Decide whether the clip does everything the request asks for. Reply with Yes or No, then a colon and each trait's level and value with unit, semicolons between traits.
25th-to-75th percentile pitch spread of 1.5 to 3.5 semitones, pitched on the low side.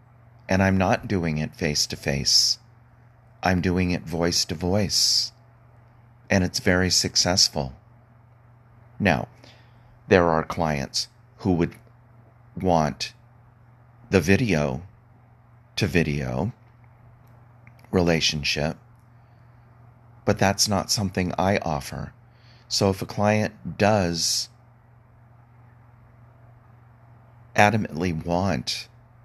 No: average, 4.2 semitones; low, 115 Hz